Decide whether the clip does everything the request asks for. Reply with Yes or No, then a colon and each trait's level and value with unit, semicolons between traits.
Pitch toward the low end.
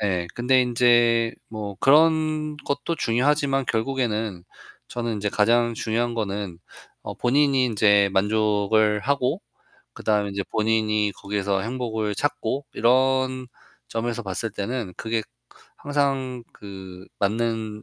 Yes: low, 115 Hz